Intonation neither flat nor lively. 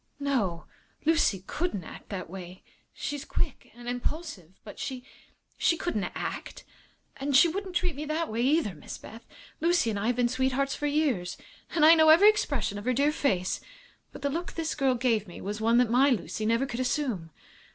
No: wide, 6.1 semitones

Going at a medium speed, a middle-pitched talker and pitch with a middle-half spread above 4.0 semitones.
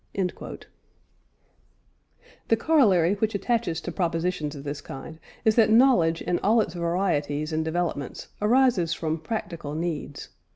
No: slow, 130 wpm; medium, 175 Hz; average, 5.1 semitones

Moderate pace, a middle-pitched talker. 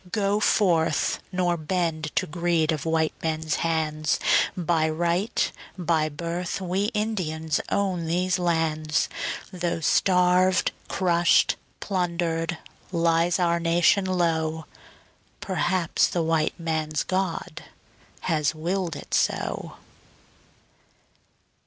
No: slow, 100 wpm; medium, 170 Hz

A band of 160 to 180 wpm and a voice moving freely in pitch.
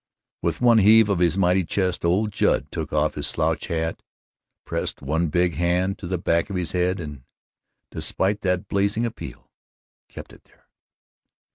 No: average, 165 wpm; average, 2.8 semitones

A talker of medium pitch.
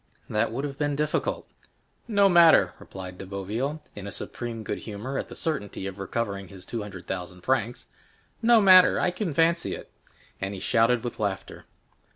No: low, 115 Hz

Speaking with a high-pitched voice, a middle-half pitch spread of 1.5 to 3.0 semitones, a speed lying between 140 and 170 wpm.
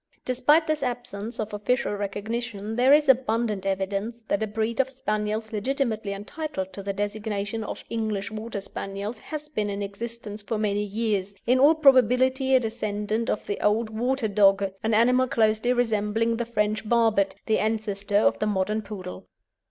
Yes: high, 220 Hz; average, 2.7 semitones; average, 165 wpm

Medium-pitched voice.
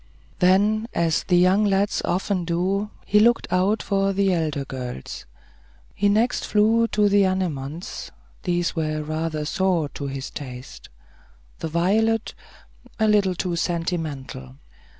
Yes: medium, 180 Hz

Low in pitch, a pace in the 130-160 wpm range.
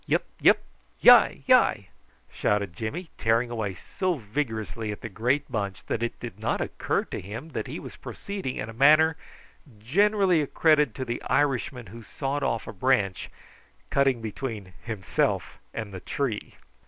Yes: low, 120 Hz; average, 155 wpm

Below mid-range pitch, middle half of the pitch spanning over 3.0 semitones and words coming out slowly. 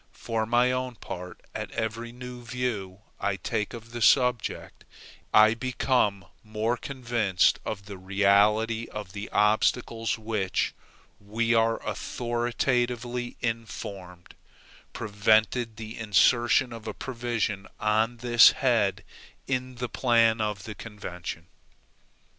No: low, 115 Hz; narrow, 2.5 semitones; slow, 115 wpm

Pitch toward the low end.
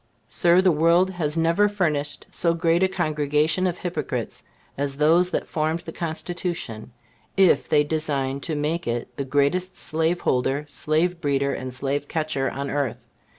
No: medium, 155 Hz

